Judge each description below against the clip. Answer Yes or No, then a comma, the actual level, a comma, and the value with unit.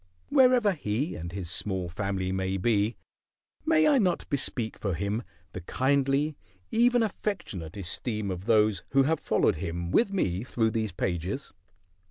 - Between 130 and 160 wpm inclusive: Yes, average, 150 wpm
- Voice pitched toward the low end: Yes, low, 110 Hz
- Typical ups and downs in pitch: No, wide, 8.1 semitones